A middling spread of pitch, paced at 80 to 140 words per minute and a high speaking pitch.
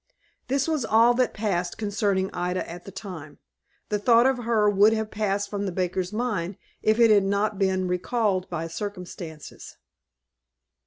No: average, 3.2 semitones; average, 160 wpm; high, 200 Hz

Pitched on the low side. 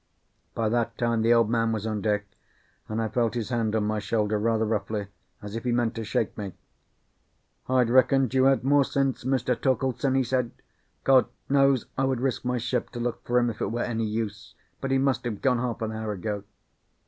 Yes: low, 115 Hz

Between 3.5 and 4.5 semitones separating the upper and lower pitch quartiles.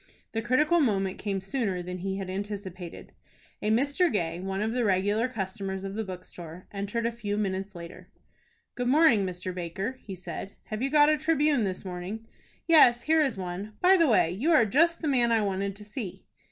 No: average, 5.0 semitones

